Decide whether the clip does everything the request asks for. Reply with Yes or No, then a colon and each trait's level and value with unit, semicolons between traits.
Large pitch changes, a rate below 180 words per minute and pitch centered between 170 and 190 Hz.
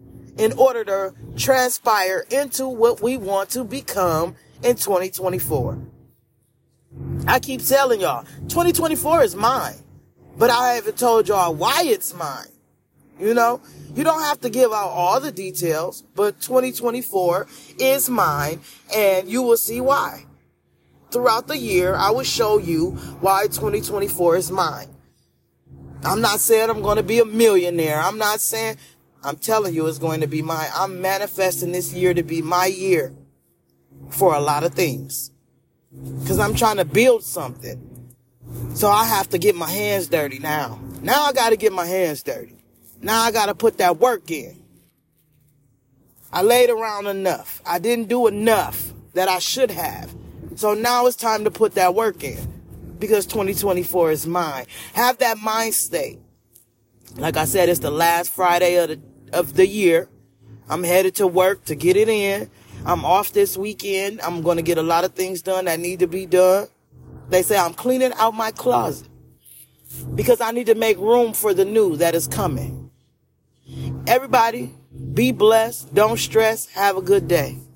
Yes: wide, 6.8 semitones; average, 165 wpm; medium, 185 Hz